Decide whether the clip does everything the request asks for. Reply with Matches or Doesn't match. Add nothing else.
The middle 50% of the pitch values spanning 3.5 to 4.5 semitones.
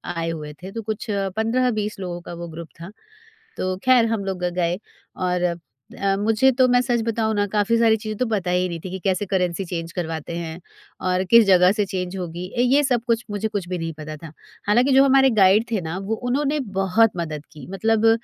Matches